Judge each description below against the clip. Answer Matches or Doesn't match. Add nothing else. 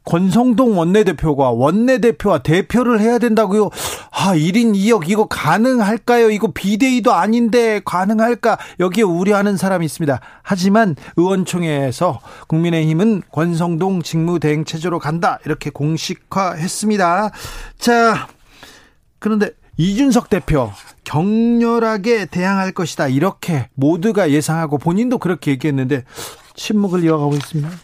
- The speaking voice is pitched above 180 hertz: Matches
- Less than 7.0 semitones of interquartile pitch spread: Matches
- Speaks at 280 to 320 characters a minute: Matches